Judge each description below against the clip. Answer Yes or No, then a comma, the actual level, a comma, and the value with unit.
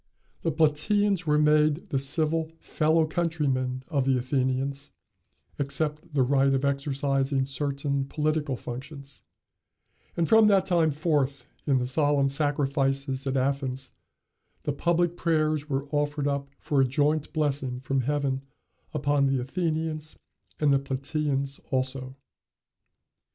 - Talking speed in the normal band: No, slow, 125 wpm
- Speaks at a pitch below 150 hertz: Yes, medium, 140 Hz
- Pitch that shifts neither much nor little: No, narrow, 2.3 semitones